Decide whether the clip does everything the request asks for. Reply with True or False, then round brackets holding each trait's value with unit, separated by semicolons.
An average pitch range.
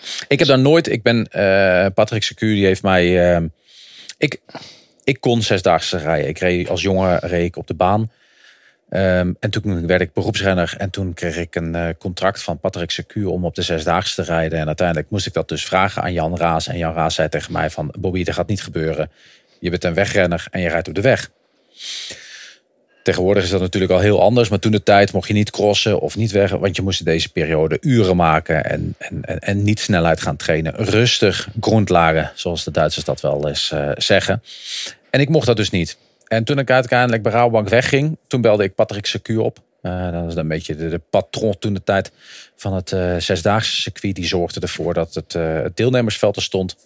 True (3.8 semitones)